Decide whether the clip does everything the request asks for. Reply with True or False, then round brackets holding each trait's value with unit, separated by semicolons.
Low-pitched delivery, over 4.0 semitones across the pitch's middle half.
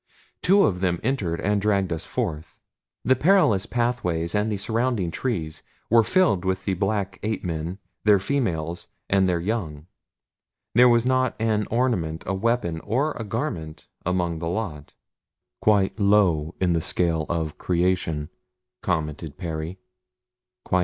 True (95 Hz; 5.1 semitones)